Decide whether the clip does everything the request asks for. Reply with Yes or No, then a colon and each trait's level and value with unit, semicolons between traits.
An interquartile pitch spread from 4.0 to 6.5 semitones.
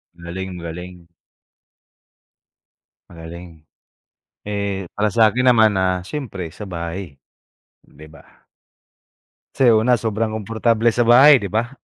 Yes: average, 4.4 semitones